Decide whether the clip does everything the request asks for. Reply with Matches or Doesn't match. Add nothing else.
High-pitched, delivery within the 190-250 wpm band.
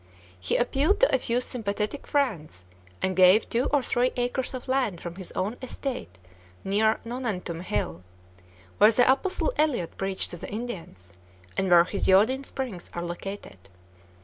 Doesn't match